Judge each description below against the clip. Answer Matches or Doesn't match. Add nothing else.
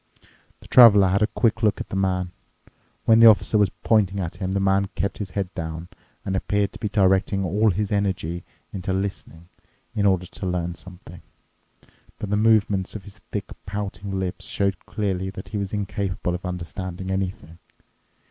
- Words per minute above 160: Matches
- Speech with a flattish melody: Matches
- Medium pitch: Doesn't match